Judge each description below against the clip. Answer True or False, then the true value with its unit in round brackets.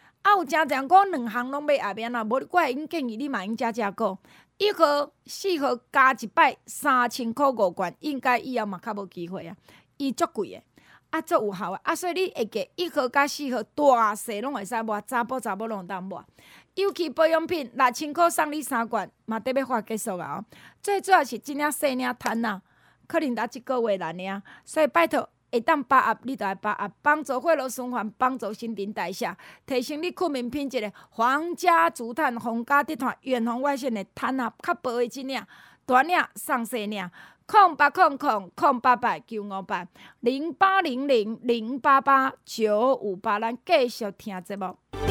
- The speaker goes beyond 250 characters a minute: True (270 characters per minute)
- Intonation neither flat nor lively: True (4.9 semitones)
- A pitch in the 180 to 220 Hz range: False (255 Hz)